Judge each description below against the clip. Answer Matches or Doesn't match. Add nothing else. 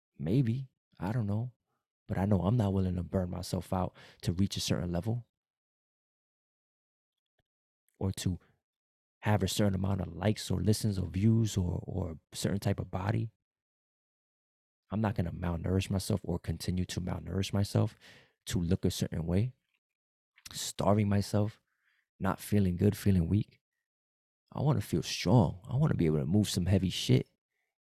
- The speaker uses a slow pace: Doesn't match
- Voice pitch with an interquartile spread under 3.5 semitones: Matches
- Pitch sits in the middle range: Doesn't match